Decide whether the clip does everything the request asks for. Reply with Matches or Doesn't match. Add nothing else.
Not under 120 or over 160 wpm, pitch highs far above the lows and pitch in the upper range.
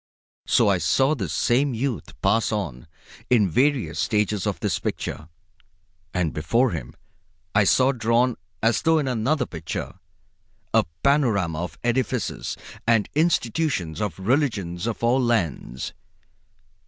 Doesn't match